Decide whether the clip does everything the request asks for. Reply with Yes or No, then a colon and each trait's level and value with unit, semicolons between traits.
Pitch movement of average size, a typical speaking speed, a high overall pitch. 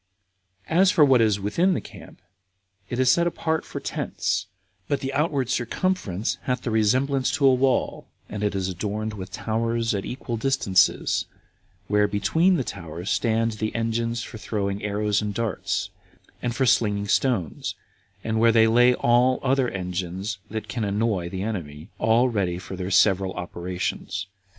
No: average, 4.3 semitones; average, 165 wpm; low, 110 Hz